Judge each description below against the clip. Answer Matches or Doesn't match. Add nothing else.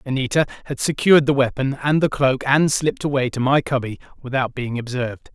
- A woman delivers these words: Doesn't match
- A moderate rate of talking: Matches